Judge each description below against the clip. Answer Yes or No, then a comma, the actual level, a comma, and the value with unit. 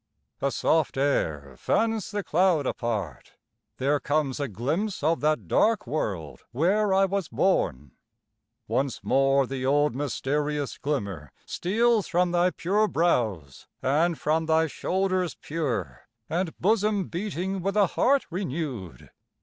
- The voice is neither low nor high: Yes, medium, 155 Hz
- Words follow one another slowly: Yes, slow, 130 wpm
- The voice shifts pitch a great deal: Yes, wide, 6.0 semitones